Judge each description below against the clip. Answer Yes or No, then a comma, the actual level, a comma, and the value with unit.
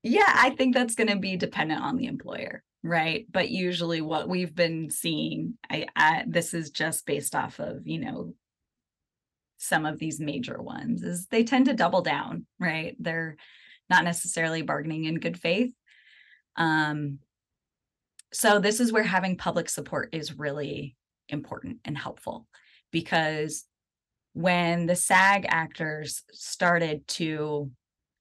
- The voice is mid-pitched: Yes, medium, 165 Hz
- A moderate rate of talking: Yes, average, 145 wpm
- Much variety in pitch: No, average, 4.5 semitones